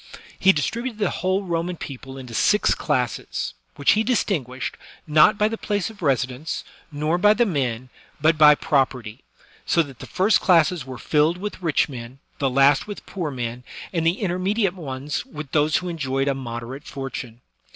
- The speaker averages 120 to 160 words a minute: No, average, 170 wpm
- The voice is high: No, medium, 150 Hz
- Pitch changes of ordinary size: No, wide, 5.7 semitones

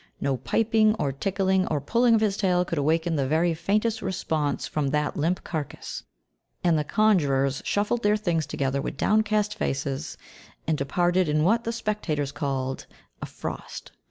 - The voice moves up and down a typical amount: No, wide, 6.4 semitones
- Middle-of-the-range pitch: Yes, medium, 170 Hz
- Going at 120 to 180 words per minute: Yes, average, 160 wpm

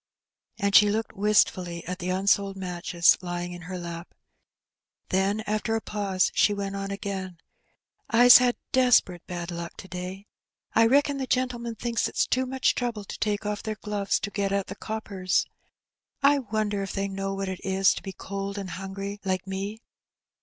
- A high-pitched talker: Yes, high, 200 Hz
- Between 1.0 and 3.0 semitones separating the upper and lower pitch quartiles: Yes, narrow, 2.5 semitones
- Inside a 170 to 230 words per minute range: Yes, average, 180 wpm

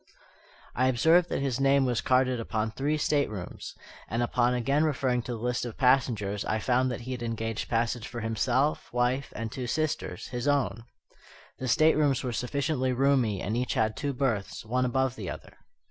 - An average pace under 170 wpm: No, average, 180 wpm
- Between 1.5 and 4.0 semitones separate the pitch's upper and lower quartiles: Yes, average, 3.0 semitones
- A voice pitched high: No, low, 125 Hz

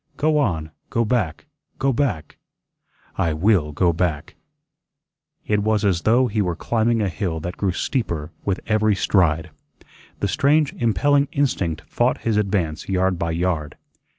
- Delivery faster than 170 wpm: No, average, 150 wpm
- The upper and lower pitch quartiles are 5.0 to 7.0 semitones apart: Yes, wide, 5.4 semitones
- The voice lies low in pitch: Yes, low, 100 Hz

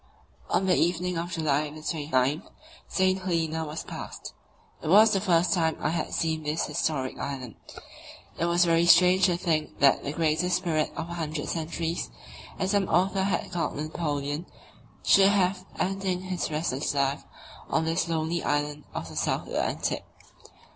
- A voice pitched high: No, medium, 165 Hz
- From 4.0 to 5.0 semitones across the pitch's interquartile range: No, average, 2.9 semitones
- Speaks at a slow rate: No, average, 160 wpm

